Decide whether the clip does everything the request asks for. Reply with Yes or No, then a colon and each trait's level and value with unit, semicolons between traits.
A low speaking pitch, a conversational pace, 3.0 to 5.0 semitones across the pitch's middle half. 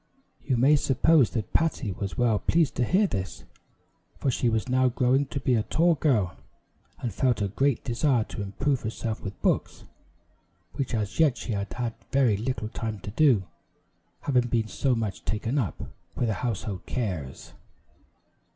Yes: low, 120 Hz; average, 170 wpm; average, 4.1 semitones